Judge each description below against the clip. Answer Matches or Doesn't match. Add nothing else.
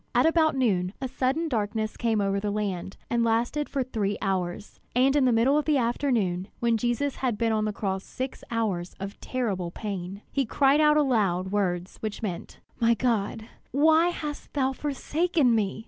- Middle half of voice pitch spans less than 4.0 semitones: Doesn't match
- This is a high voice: Matches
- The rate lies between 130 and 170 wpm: Doesn't match